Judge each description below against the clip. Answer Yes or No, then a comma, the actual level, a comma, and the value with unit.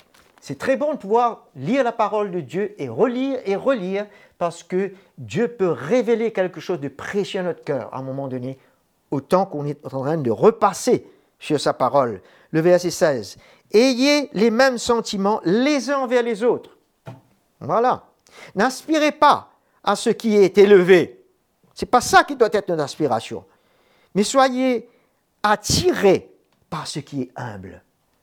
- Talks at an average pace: Yes, average, 165 wpm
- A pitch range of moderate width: No, wide, 6.8 semitones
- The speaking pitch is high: Yes, high, 205 Hz